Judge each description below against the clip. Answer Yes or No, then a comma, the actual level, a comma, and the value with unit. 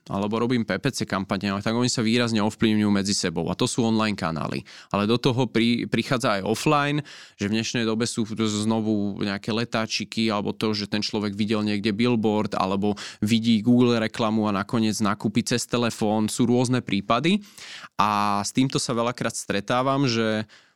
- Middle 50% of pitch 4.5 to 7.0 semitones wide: No, narrow, 2.5 semitones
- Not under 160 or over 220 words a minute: Yes, fast, 165 wpm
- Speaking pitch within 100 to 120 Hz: Yes, low, 110 Hz